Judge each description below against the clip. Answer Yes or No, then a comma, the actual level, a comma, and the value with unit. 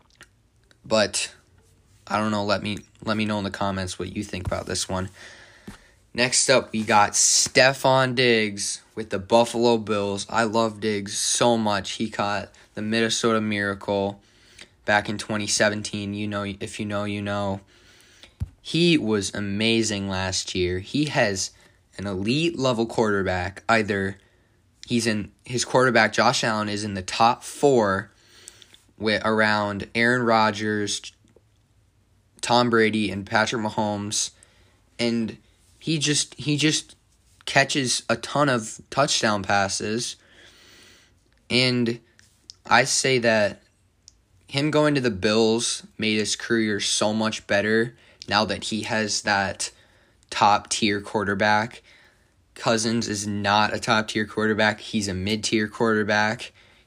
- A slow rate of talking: Yes, slow, 130 wpm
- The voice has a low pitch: Yes, low, 105 Hz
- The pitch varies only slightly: Yes, narrow, 2.3 semitones